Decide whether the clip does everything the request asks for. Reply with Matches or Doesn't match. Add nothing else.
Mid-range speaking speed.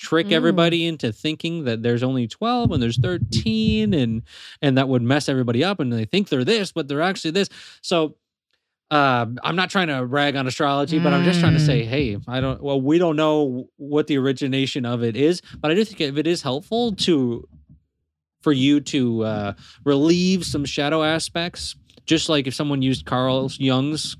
Matches